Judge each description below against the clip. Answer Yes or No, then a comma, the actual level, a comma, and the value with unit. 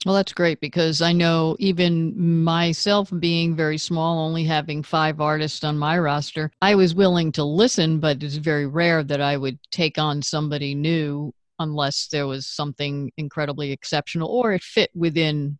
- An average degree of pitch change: No, narrow, 2.3 semitones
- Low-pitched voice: No, medium, 155 Hz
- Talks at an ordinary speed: Yes, average, 170 wpm